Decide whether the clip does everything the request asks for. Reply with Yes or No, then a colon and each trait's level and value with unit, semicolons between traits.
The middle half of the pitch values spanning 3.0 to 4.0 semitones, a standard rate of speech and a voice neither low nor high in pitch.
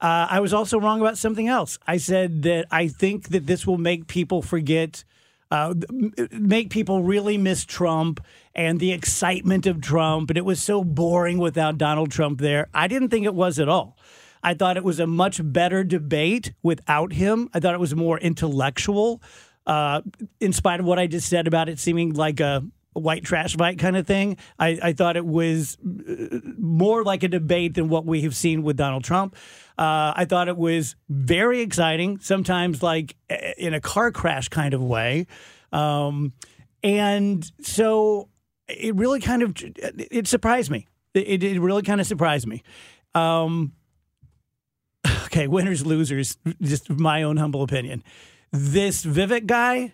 Yes: average, 3.7 semitones; average, 170 wpm; medium, 170 Hz